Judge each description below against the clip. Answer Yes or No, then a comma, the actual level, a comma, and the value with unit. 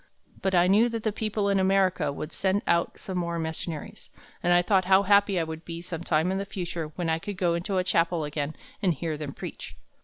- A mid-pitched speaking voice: Yes, medium, 180 Hz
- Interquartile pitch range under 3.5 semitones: Yes, average, 2.8 semitones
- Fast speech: Yes, fast, 225 wpm